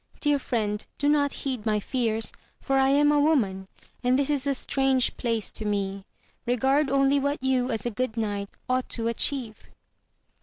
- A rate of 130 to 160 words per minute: No, average, 180 wpm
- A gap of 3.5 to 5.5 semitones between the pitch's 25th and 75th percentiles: Yes, average, 4.0 semitones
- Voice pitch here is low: No, very high, 255 Hz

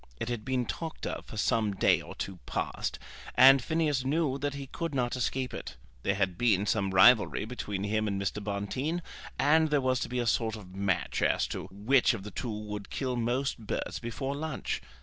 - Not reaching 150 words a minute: No, fast, 205 wpm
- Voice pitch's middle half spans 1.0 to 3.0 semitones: No, average, 4.8 semitones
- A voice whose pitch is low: Yes, low, 120 Hz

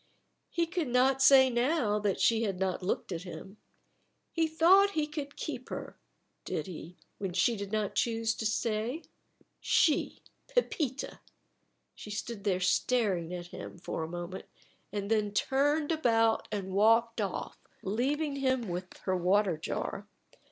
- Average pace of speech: Yes, average, 150 wpm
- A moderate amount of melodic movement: No, wide, 6.0 semitones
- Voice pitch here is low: No, high, 225 Hz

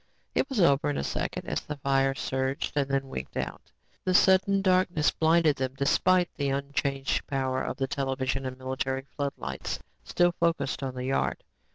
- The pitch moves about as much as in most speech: Yes, average, 3.7 semitones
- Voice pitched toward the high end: No, medium, 140 Hz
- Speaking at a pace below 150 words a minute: No, average, 175 wpm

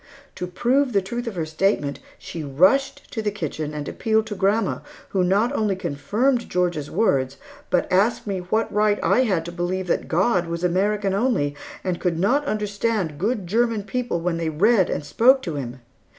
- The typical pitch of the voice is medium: No, high, 195 Hz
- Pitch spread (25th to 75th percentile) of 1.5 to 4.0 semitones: No, average, 4.7 semitones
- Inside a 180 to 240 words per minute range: Yes, average, 185 wpm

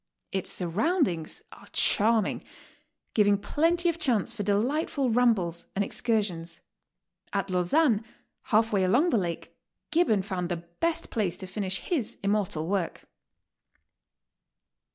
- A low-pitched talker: No, high, 205 Hz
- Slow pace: Yes, slow, 120 wpm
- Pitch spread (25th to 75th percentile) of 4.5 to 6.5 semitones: Yes, average, 5.1 semitones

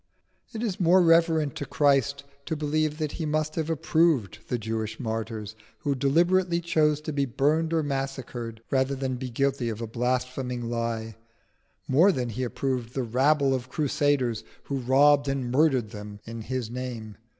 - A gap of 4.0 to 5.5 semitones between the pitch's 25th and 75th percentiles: Yes, average, 4.3 semitones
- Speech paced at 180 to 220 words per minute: No, average, 165 wpm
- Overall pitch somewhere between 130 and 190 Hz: Yes, low, 135 Hz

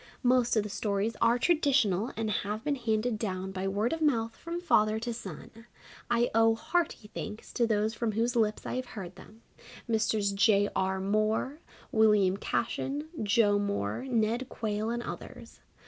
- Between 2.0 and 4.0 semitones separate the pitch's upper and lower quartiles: Yes, narrow, 2.6 semitones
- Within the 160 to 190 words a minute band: Yes, average, 165 wpm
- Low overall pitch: No, high, 220 Hz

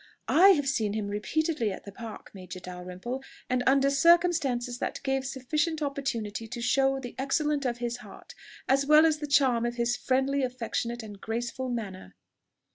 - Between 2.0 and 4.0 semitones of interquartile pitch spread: Yes, average, 3.3 semitones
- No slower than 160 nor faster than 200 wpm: Yes, average, 170 wpm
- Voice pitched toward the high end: Yes, very high, 255 Hz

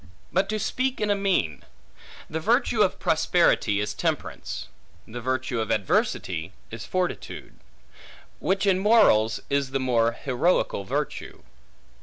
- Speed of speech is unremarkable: No, slow, 130 wpm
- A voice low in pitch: Yes, low, 130 Hz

